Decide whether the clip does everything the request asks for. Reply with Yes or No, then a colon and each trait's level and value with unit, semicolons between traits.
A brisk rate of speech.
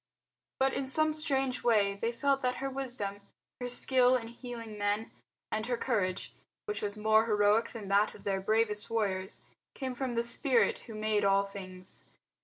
No: average, 175 wpm